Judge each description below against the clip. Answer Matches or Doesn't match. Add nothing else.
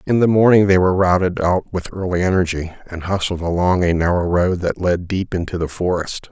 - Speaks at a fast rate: Matches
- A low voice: Matches